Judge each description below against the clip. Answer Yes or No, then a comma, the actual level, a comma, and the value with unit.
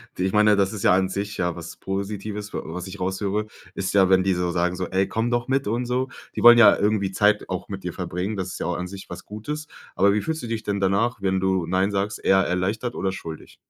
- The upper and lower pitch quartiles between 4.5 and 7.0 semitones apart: No, narrow, 2.4 semitones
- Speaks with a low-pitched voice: Yes, low, 100 Hz